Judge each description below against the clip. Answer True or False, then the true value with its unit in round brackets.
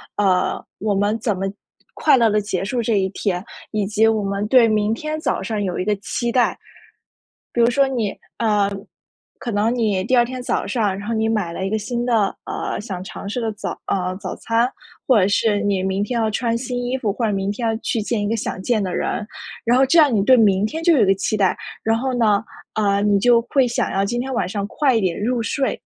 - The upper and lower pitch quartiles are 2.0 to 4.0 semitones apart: True (3.1 semitones)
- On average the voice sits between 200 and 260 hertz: True (220 Hz)